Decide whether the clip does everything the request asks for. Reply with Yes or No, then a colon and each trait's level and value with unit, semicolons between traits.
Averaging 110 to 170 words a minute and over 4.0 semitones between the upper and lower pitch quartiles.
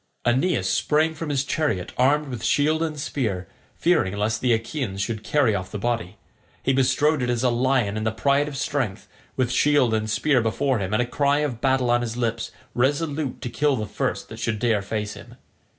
No: fast, 205 wpm; average, 4.4 semitones